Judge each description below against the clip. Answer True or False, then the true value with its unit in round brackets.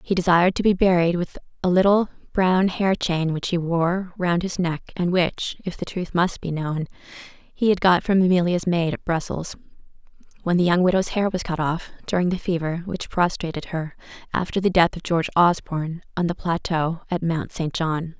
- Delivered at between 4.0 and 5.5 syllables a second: True (5.1 syllables/s)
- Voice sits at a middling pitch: True (175 Hz)